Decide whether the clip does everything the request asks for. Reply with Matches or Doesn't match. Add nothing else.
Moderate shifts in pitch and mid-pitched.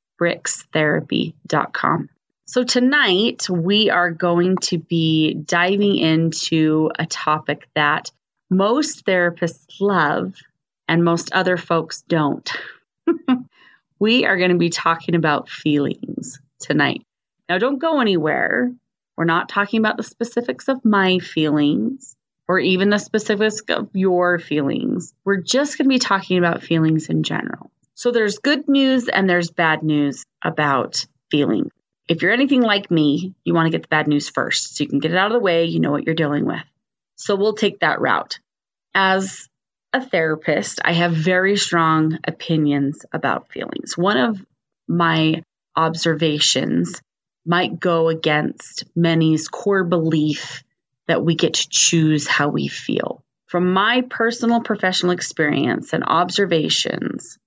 Matches